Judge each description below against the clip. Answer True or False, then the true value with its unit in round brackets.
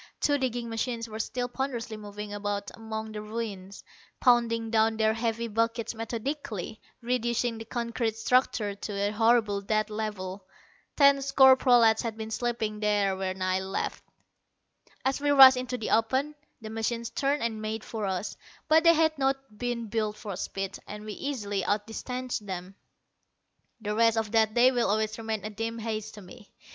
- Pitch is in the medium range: False (225 Hz)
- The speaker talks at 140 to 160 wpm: False (170 wpm)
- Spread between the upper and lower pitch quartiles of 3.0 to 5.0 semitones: False (2.5 semitones)